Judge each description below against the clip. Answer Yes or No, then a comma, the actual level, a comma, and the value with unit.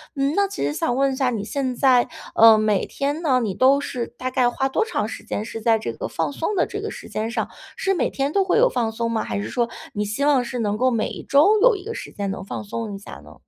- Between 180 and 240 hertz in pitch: No, very high, 255 Hz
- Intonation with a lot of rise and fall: No, average, 4.5 semitones